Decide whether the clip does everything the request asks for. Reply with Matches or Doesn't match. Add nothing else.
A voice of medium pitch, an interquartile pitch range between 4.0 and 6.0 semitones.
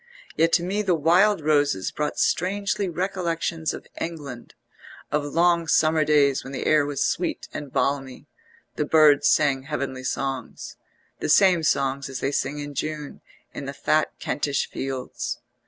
Doesn't match